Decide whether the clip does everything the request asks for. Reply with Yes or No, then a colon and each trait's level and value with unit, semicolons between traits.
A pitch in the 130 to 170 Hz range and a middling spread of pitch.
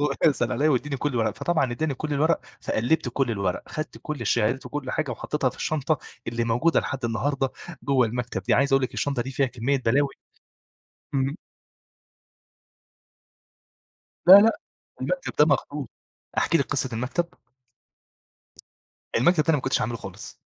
Yes: low, 135 Hz; average, 3.8 semitones